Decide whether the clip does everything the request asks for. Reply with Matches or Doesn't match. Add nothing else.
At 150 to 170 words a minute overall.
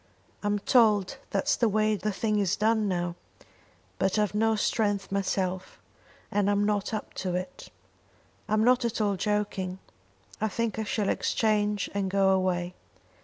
Matches